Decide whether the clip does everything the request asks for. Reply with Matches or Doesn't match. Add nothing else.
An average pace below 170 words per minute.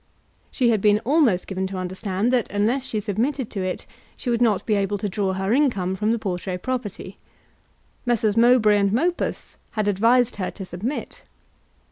Doesn't match